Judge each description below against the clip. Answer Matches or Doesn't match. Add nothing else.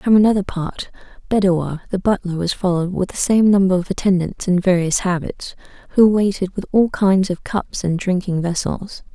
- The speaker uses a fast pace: Doesn't match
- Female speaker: Matches